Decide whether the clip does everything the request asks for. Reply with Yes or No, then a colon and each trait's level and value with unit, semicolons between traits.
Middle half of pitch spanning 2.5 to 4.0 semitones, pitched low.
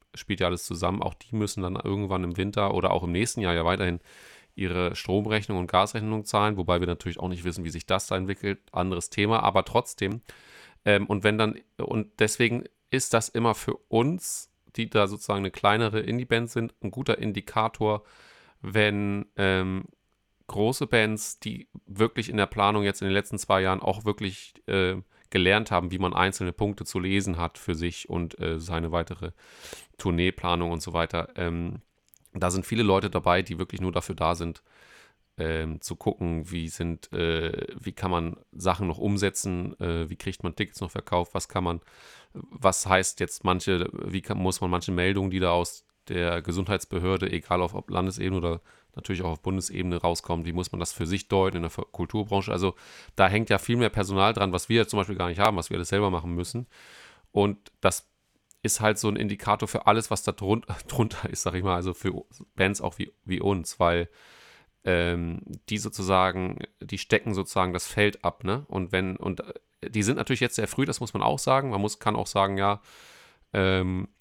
Yes: average, 2.8 semitones; very low, 95 Hz